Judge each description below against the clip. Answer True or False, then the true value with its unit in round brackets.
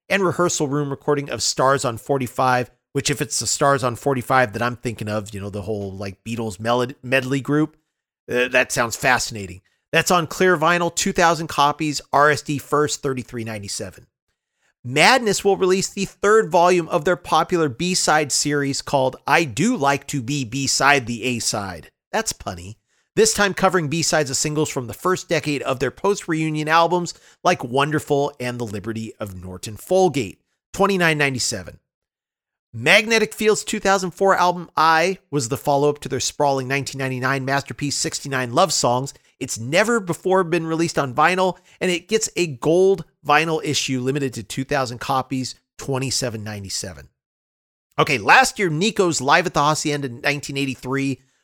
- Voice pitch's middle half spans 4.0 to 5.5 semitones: True (5.1 semitones)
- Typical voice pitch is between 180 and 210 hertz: False (140 Hz)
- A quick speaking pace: False (150 wpm)